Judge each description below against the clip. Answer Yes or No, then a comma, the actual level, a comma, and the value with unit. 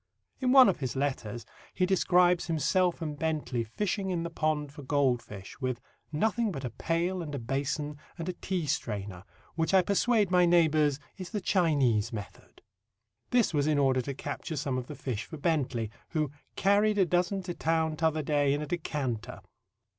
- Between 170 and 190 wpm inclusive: Yes, average, 180 wpm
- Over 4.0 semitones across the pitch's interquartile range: Yes, average, 4.9 semitones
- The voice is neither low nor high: Yes, medium, 155 Hz